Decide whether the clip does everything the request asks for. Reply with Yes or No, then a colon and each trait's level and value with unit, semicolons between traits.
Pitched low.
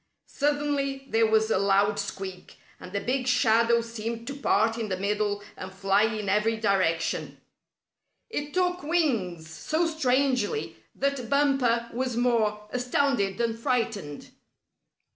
No: high, 230 Hz